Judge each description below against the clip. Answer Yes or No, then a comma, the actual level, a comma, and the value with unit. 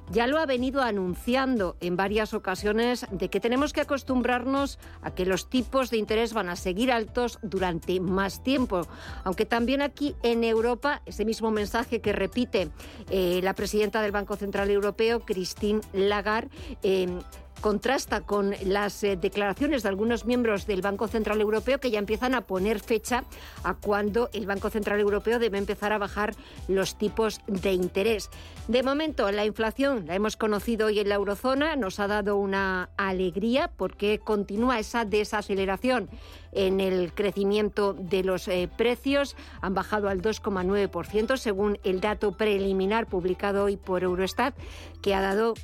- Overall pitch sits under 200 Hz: No, high, 210 Hz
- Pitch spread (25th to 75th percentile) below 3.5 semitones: Yes, average, 3.1 semitones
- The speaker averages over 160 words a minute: No, average, 155 wpm